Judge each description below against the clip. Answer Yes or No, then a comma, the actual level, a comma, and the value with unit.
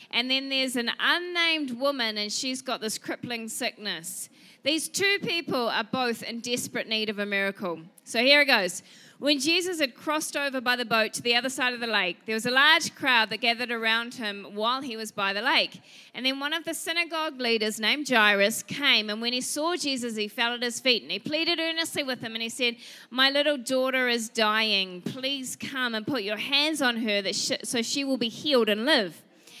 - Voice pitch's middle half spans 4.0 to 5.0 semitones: Yes, average, 4.3 semitones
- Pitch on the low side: No, high, 245 Hz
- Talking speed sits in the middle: No, fast, 220 wpm